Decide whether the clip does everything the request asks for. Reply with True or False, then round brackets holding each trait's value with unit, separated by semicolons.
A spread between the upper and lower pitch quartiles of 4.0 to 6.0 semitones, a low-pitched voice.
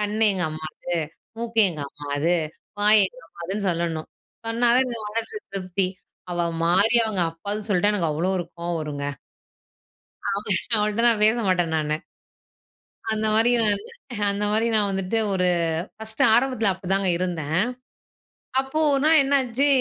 False (4.5 semitones; 200 Hz)